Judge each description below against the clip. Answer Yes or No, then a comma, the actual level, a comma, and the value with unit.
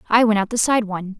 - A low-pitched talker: No, high, 215 Hz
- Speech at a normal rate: No, fast, 300 wpm